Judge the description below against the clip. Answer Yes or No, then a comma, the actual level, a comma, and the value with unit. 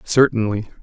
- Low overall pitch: Yes, low, 115 Hz